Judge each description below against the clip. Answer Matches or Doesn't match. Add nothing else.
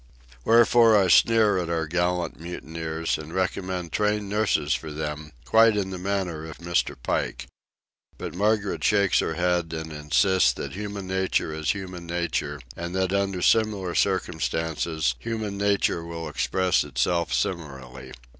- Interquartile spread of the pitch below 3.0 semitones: Doesn't match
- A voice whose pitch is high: Doesn't match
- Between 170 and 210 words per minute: Doesn't match